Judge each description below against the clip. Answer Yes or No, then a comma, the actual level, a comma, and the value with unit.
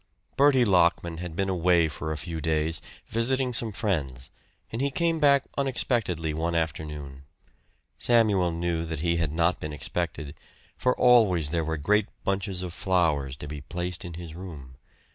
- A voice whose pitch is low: Yes, very low, 85 Hz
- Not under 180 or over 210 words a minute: No, average, 160 wpm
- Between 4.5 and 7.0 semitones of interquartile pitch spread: Yes, average, 4.8 semitones